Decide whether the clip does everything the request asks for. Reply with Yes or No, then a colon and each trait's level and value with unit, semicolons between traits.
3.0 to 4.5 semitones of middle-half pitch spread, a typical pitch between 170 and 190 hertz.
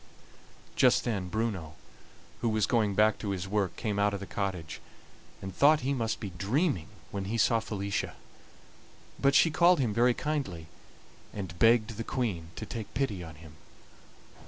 No: average, 3.8 semitones; low, 105 Hz